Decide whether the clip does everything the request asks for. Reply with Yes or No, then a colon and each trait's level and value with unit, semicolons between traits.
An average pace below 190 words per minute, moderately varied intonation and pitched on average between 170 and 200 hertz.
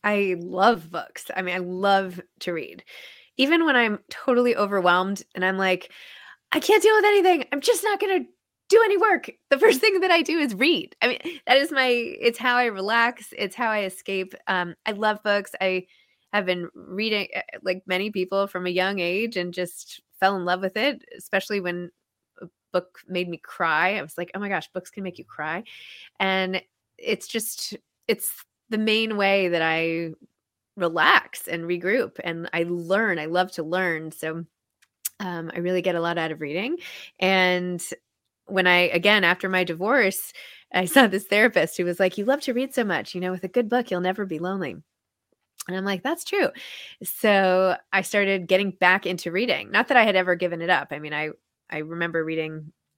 No: average, 200 wpm; average, 4.6 semitones; high, 190 Hz